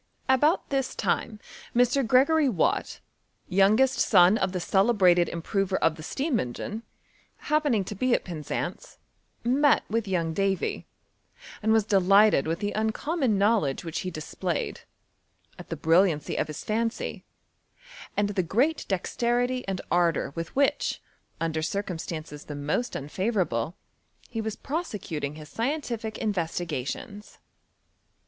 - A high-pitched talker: Yes, high, 200 Hz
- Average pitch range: No, wide, 6.0 semitones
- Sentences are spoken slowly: Yes, slow, 130 wpm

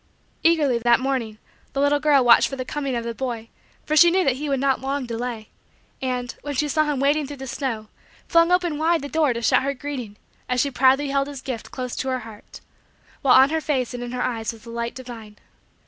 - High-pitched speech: Yes, very high, 265 Hz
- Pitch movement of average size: Yes, average, 3.1 semitones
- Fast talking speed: Yes, fast, 235 wpm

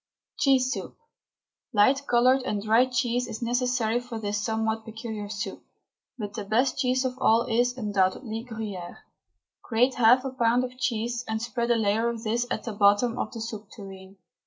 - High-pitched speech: Yes, high, 230 Hz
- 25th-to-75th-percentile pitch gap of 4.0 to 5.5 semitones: No, narrow, 2.5 semitones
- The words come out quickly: No, average, 175 wpm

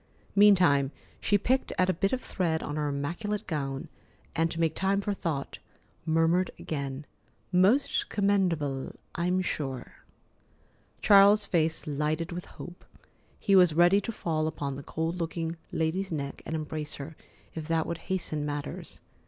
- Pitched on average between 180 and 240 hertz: No, medium, 165 Hz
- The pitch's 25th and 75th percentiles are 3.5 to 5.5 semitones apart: Yes, average, 3.8 semitones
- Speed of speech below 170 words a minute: Yes, average, 150 wpm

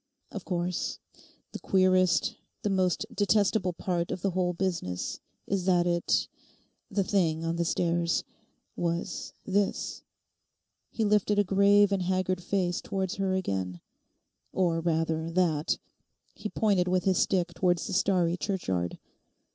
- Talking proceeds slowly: Yes, slow, 125 wpm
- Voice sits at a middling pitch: Yes, medium, 180 Hz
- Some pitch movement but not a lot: No, narrow, 2.2 semitones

